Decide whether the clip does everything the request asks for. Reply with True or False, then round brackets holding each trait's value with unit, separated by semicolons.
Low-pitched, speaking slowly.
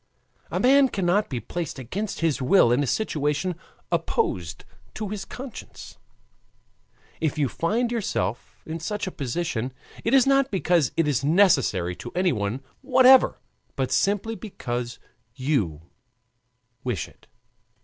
False (165 Hz; 130 wpm)